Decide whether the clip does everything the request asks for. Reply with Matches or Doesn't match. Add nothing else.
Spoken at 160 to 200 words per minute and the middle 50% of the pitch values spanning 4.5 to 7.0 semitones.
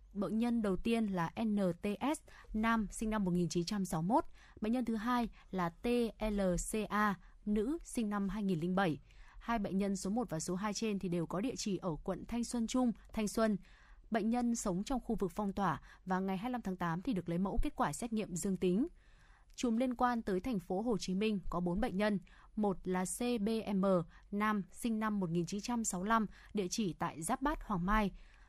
Doesn't match